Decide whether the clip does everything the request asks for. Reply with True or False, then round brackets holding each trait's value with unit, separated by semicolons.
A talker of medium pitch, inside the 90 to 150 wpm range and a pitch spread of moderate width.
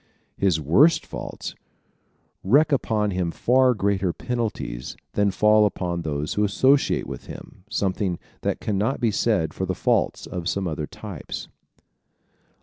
False (100 Hz; 145 wpm; 4.5 semitones)